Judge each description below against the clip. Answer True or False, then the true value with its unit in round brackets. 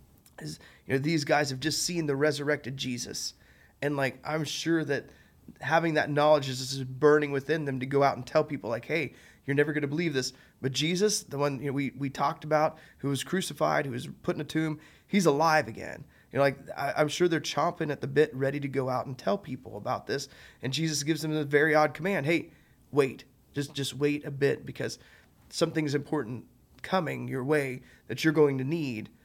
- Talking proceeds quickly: True (215 wpm)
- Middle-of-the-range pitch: True (145 Hz)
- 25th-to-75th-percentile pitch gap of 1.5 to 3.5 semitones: True (2.9 semitones)